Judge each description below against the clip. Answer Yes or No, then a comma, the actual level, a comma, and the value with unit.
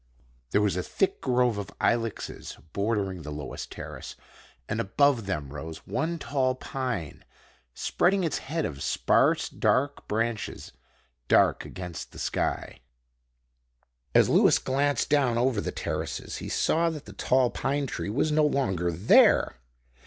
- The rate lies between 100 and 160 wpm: Yes, average, 140 wpm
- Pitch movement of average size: No, wide, 6.8 semitones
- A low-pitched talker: Yes, low, 120 Hz